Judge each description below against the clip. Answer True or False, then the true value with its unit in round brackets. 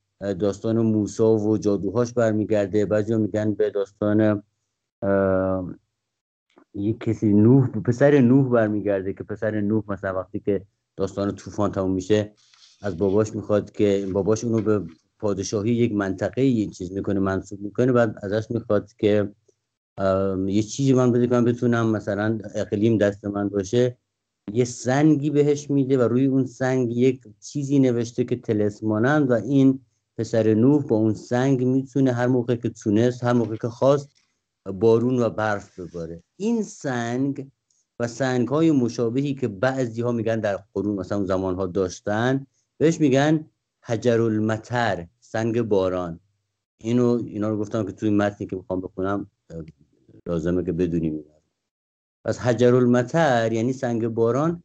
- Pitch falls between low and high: False (110 Hz)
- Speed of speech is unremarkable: True (145 wpm)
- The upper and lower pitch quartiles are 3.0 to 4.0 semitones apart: True (3.5 semitones)